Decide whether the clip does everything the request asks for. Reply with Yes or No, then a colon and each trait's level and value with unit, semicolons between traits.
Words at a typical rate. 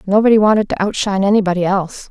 Yes: average, 170 wpm